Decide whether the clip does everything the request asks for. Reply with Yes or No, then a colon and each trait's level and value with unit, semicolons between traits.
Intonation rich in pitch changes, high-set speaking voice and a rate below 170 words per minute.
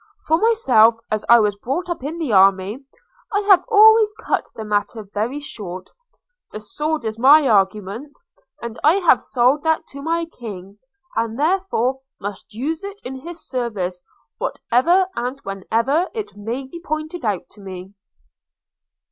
Yes: wide, 7.5 semitones; very high, 255 Hz; average, 155 wpm